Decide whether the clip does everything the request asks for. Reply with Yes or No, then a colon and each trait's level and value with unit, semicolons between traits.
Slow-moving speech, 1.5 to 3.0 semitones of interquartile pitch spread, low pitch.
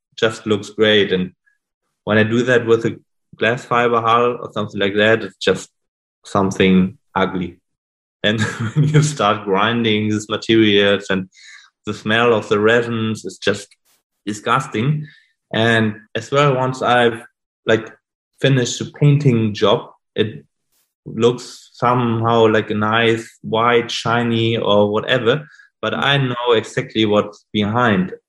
Yes: slow, 130 wpm; narrow, 2.4 semitones; low, 115 Hz